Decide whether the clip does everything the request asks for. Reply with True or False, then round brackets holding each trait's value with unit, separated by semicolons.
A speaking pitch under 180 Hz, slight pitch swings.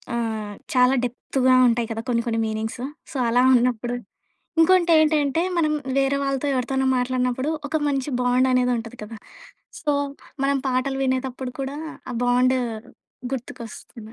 False (255 Hz; 2.2 semitones)